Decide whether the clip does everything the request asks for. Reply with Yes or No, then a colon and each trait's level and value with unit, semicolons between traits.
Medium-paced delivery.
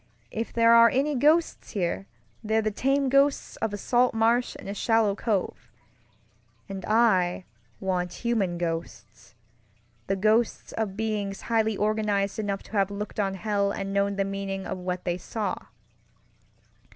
Yes: average, 150 wpm